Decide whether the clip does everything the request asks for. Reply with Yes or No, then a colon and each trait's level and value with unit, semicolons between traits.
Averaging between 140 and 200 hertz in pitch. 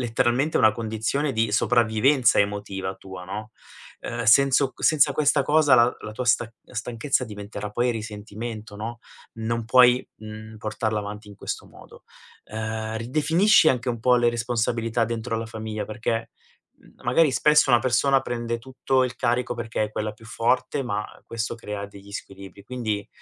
No: low, 115 Hz